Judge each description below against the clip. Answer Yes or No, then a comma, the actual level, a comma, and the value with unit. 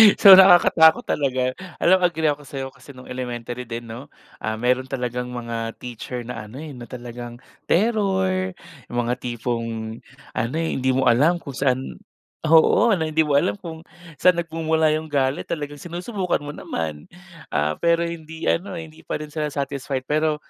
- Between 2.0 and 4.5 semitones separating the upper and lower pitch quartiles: No, average, 4.9 semitones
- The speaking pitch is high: No, medium, 140 Hz